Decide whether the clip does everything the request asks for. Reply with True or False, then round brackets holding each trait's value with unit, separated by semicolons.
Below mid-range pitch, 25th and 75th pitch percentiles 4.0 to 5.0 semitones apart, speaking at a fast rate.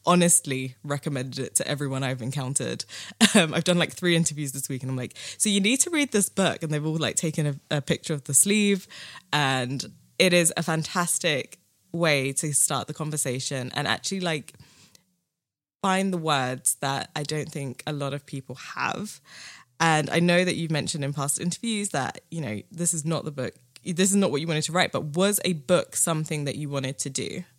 False (155 Hz; 4.3 semitones; 210 wpm)